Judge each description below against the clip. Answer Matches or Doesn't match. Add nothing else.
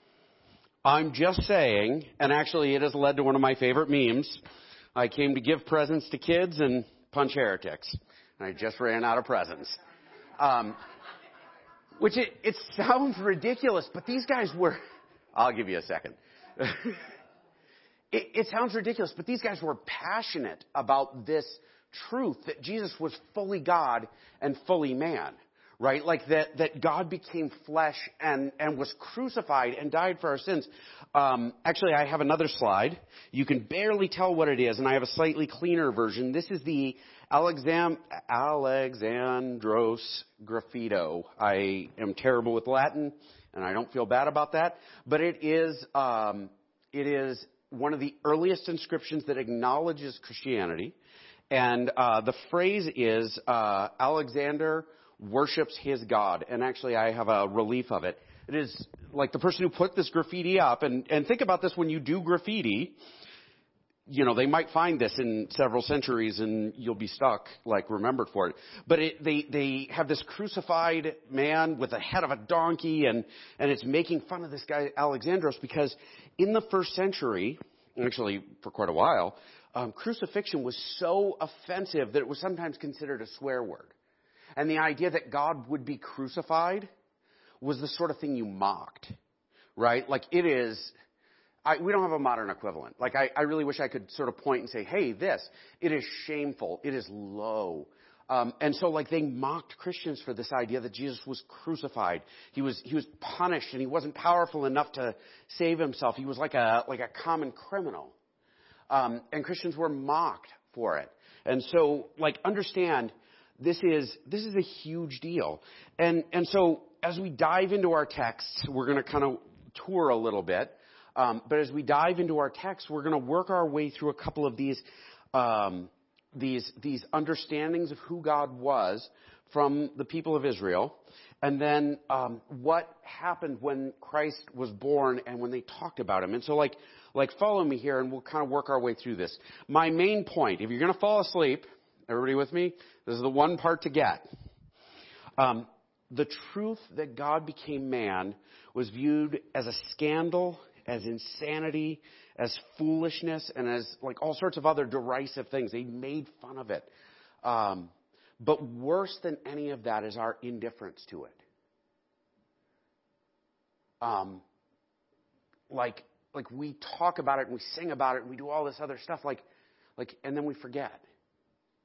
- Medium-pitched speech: Matches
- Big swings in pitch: Doesn't match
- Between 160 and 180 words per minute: Matches